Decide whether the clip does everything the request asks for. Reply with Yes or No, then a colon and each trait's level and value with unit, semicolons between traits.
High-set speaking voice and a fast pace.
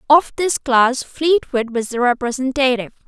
No: very high, 260 Hz; slow, 135 wpm